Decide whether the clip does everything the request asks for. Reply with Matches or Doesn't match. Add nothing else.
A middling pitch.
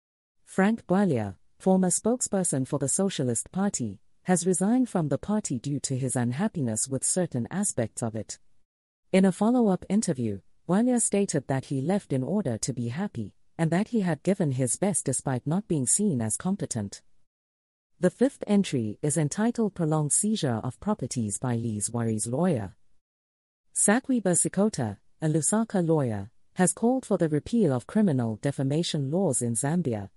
Matches